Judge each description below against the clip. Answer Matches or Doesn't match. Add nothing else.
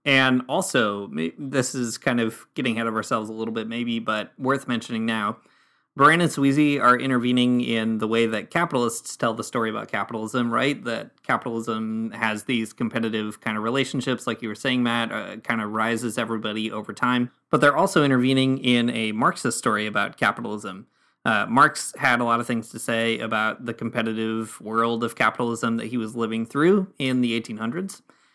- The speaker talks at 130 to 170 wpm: Doesn't match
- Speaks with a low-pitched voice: Matches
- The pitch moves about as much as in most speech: Doesn't match